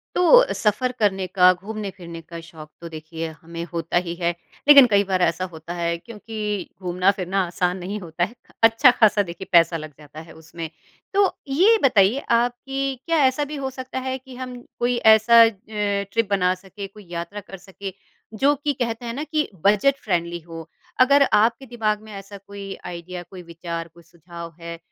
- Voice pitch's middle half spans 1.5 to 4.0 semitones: No, wide, 5.5 semitones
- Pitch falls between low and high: No, high, 195 Hz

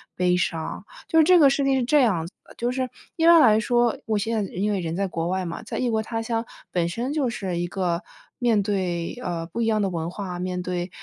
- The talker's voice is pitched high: Yes, high, 205 Hz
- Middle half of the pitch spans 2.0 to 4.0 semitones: No, average, 5.1 semitones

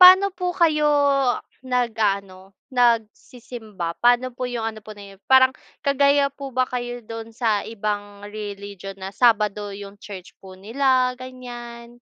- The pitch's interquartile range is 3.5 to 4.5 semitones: Yes, average, 3.9 semitones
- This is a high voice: Yes, high, 230 Hz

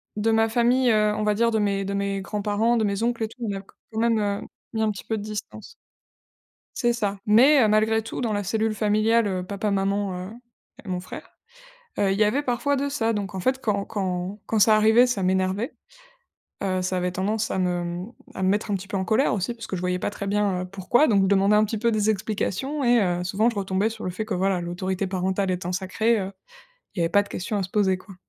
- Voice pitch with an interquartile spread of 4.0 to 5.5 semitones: No, average, 2.8 semitones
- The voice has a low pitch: No, high, 205 Hz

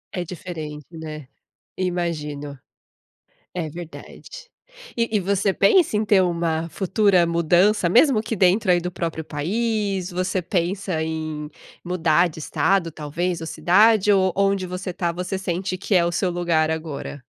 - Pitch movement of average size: Yes, average, 3.2 semitones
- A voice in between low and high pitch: Yes, medium, 175 Hz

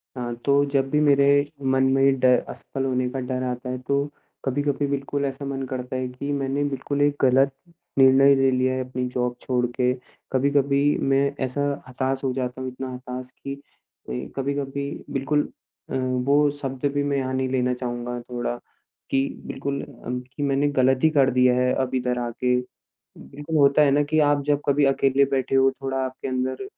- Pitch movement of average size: No, narrow, 1.7 semitones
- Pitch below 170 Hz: Yes, low, 135 Hz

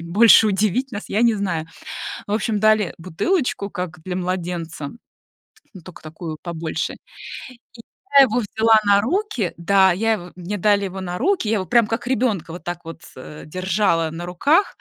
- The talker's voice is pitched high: Yes, high, 195 Hz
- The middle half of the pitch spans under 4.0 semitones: No, average, 4.3 semitones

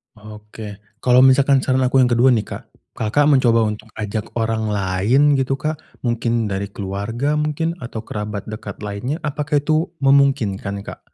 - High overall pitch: No, low, 115 Hz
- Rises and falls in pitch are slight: No, average, 4.8 semitones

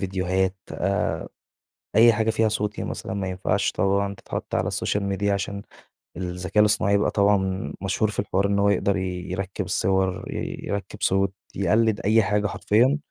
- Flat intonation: Yes, narrow, 1.7 semitones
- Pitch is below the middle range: Yes, low, 100 Hz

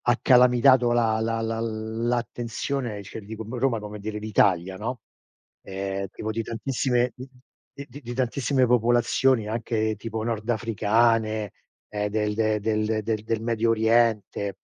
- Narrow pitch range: Yes, narrow, 1.9 semitones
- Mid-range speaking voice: No, low, 115 Hz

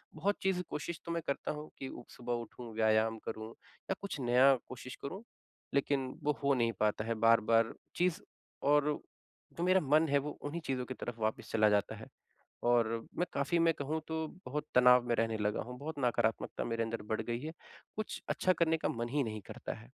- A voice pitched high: No, low, 130 Hz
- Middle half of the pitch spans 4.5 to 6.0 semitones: Yes, average, 5.3 semitones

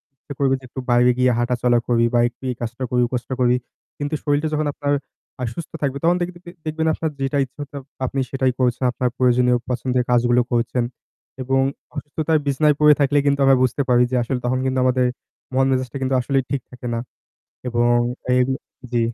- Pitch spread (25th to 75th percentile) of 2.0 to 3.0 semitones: Yes, narrow, 2.4 semitones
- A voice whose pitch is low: Yes, low, 130 Hz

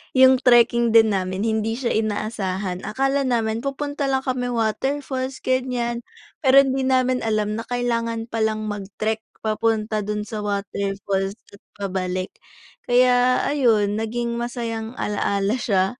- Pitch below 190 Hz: No, high, 225 Hz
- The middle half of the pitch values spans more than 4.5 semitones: No, average, 3.2 semitones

